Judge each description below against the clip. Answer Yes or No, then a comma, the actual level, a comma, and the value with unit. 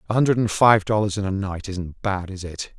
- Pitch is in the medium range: No, low, 100 Hz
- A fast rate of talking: Yes, fast, 260 wpm